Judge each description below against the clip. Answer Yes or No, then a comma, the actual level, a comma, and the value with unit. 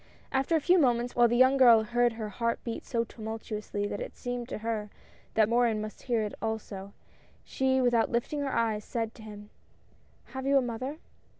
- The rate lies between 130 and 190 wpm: No, average, 200 wpm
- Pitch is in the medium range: No, high, 235 Hz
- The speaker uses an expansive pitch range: No, narrow, 2.6 semitones